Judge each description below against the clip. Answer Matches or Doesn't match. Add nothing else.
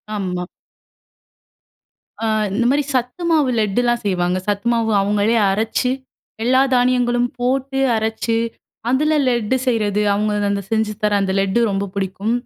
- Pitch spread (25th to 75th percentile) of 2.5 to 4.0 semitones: Matches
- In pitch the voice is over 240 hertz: Doesn't match